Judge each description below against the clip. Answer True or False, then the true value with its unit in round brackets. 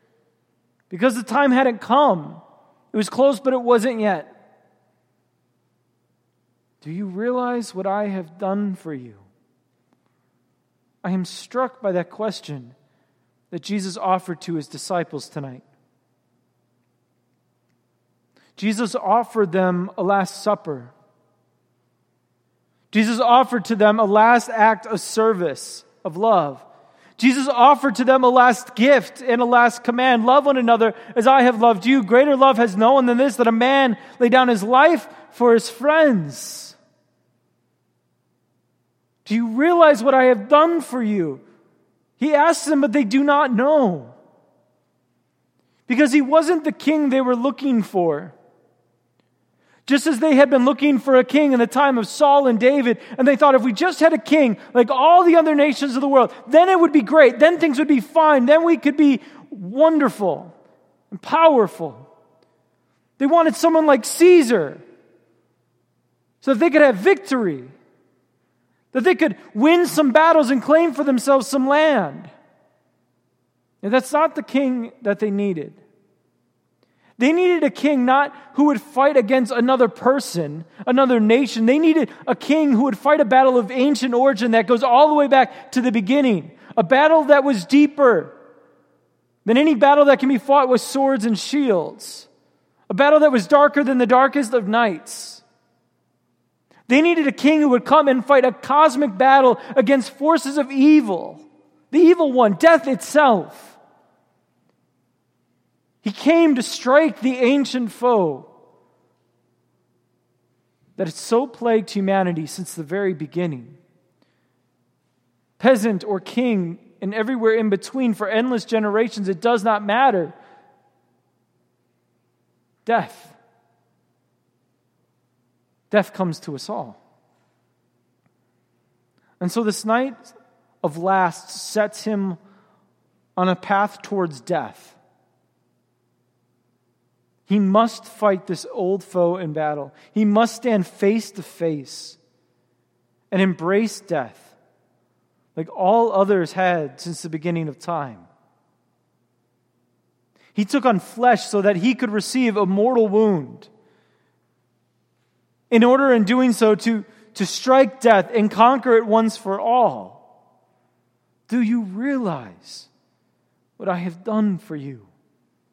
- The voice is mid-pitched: False (230 Hz)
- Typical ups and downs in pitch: False (6.9 semitones)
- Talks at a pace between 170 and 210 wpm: False (140 wpm)